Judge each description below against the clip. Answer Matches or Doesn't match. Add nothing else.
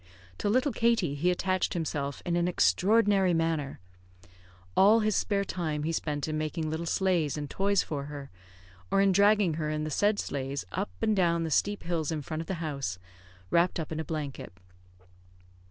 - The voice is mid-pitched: Matches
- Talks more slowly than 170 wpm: Doesn't match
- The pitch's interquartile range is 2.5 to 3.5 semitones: Doesn't match